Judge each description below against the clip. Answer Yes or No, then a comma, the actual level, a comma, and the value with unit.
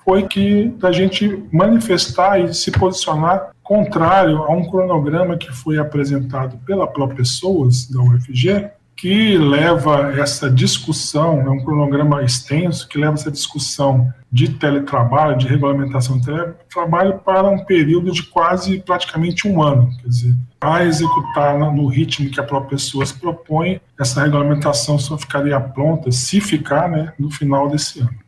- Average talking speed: Yes, average, 145 wpm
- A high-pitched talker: No, medium, 150 Hz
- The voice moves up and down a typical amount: Yes, average, 4.1 semitones